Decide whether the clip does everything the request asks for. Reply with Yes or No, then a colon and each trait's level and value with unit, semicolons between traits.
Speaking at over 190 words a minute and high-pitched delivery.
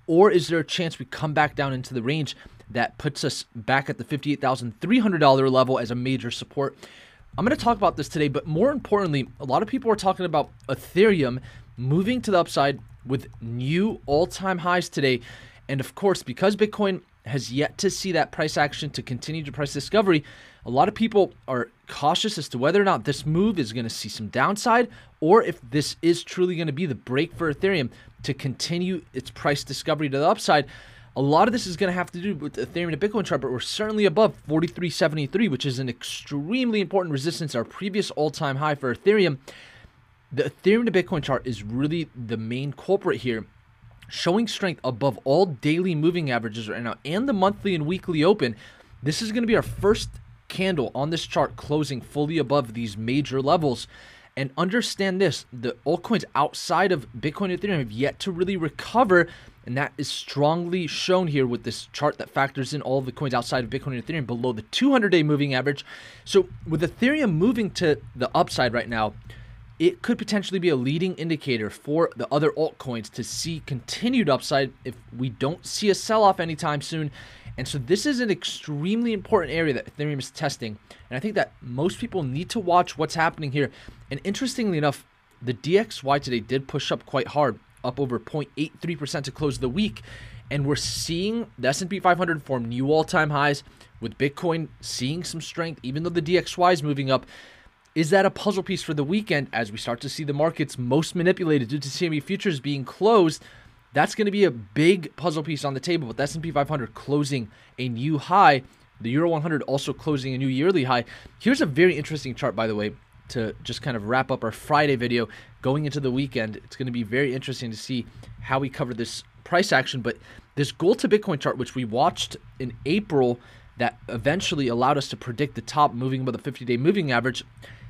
No: average, 200 wpm; medium, 145 Hz